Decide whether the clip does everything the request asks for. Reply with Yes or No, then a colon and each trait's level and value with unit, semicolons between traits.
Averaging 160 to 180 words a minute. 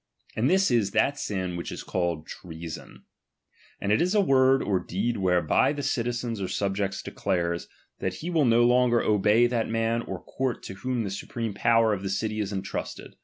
No: average, 190 wpm